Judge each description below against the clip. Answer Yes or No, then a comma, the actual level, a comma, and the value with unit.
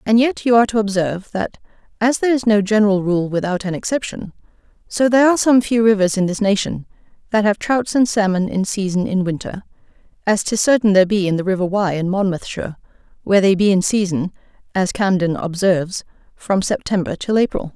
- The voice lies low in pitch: No, high, 200 Hz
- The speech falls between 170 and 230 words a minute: Yes, average, 195 wpm